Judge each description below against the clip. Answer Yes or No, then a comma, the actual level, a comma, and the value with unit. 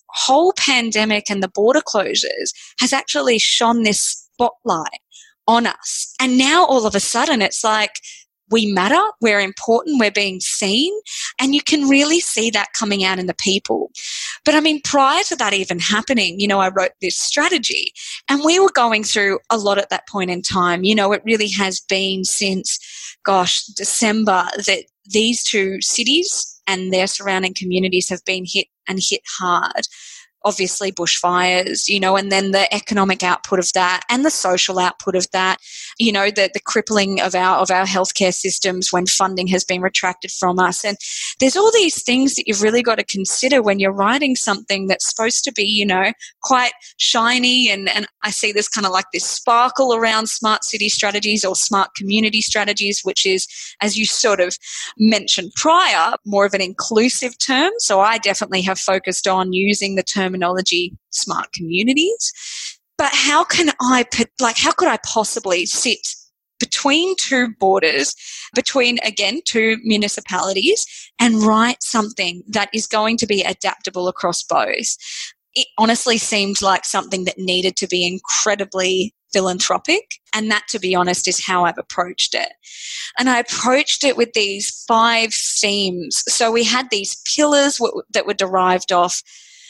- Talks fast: No, average, 170 wpm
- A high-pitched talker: Yes, high, 210 Hz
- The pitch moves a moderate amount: Yes, average, 4.7 semitones